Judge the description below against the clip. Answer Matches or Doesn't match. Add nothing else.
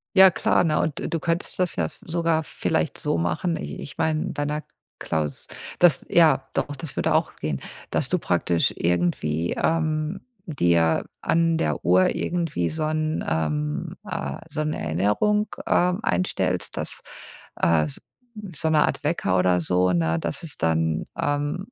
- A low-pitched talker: Doesn't match